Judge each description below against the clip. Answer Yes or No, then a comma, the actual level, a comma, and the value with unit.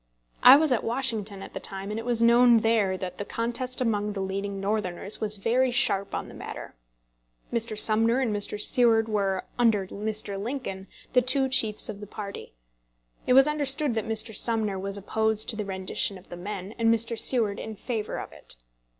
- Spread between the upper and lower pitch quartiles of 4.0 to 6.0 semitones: No, average, 2.9 semitones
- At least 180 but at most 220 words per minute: Yes, average, 195 wpm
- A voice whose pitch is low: No, high, 220 Hz